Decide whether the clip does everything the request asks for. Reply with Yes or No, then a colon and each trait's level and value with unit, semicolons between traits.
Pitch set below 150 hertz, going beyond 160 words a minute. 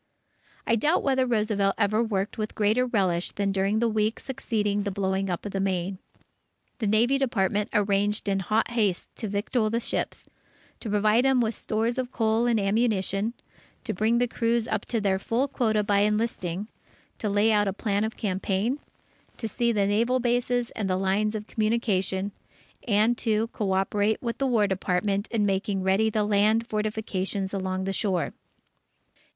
No: high, 210 Hz; average, 175 wpm